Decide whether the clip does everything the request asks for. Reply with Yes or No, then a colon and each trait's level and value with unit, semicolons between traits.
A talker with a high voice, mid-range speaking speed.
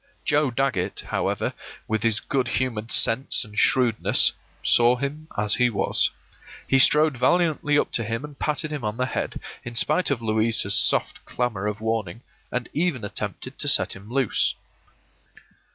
No: low, 125 Hz; average, 160 wpm